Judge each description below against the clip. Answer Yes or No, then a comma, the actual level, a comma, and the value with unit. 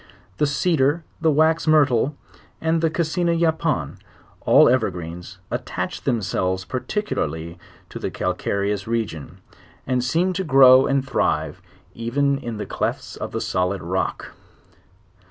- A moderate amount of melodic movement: No, wide, 8.6 semitones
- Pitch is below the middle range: Yes, low, 130 Hz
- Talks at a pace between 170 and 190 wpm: No, slow, 135 wpm